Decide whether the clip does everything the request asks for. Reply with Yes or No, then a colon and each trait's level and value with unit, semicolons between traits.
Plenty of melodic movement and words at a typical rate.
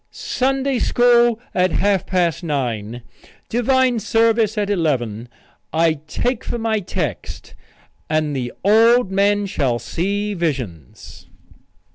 No: wide, 7.8 semitones; slow, 110 wpm